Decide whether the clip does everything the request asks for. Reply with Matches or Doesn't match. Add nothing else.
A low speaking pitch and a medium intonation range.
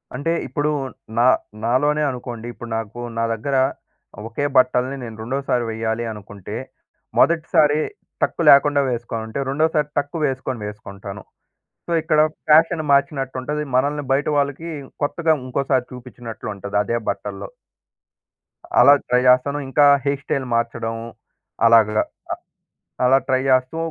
Matches